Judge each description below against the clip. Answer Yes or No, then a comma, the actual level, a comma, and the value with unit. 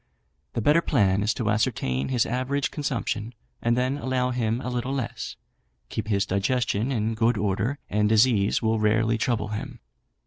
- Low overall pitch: Yes, low, 115 Hz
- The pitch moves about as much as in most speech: Yes, average, 3.2 semitones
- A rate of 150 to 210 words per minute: Yes, average, 165 wpm